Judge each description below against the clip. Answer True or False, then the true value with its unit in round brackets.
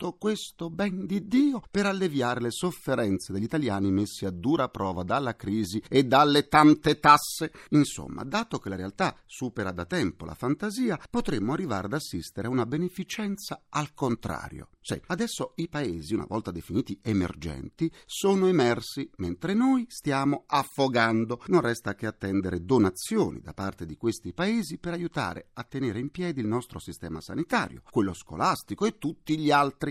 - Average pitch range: False (9.0 semitones)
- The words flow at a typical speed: True (160 wpm)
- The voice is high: False (135 Hz)